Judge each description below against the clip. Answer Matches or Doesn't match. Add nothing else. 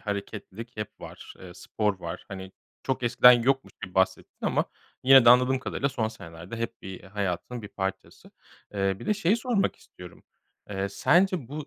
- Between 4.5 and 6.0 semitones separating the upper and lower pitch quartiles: Matches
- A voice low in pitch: Matches